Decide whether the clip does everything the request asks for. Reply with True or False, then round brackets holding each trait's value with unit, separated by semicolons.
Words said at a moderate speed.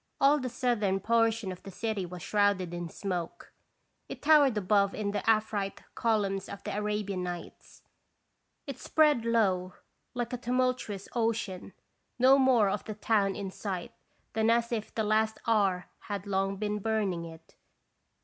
True (155 wpm)